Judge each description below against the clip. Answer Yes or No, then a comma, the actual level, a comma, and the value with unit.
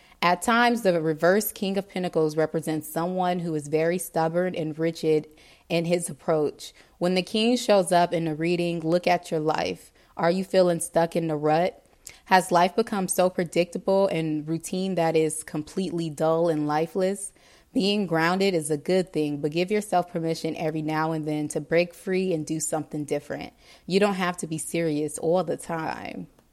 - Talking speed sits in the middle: Yes, average, 180 wpm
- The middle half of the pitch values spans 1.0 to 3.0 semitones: Yes, narrow, 2.6 semitones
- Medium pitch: Yes, medium, 170 Hz